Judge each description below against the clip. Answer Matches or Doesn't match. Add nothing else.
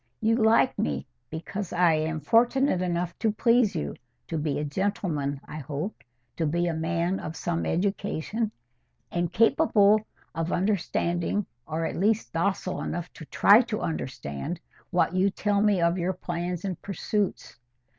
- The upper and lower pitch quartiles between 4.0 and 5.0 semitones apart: Matches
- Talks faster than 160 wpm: Doesn't match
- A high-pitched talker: Doesn't match